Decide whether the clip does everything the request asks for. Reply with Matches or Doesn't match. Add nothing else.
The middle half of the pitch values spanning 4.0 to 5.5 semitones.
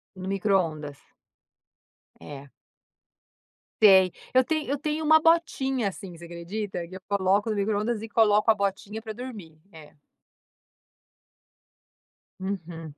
Matches